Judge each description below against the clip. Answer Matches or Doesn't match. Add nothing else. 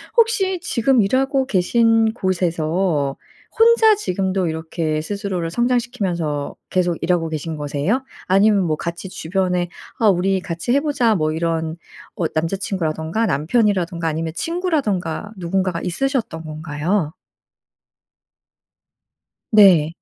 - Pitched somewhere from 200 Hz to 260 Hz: Doesn't match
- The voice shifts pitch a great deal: Matches